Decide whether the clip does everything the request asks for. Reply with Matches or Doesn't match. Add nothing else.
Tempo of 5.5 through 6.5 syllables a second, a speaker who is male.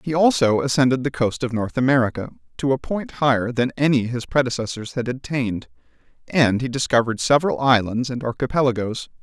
Matches